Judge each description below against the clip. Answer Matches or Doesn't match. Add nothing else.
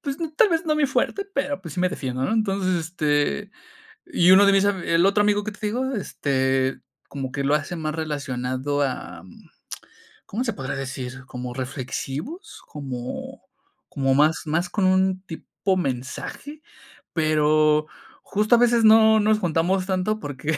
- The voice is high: Doesn't match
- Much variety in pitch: Matches